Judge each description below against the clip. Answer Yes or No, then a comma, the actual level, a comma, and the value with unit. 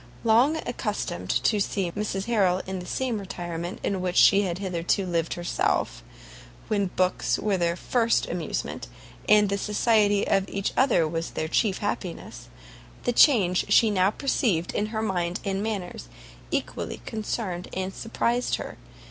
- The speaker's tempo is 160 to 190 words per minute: No, average, 150 wpm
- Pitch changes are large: No, average, 3.3 semitones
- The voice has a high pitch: Yes, high, 195 Hz